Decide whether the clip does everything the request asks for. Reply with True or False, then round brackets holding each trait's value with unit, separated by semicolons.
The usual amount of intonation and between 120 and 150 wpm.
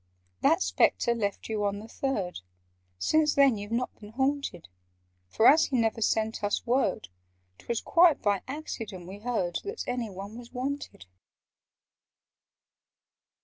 True (4.8 semitones; 140 wpm)